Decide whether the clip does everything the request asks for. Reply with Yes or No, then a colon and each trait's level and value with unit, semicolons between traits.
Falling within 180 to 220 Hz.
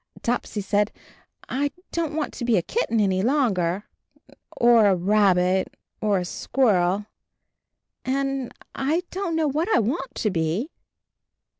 No: high, 230 Hz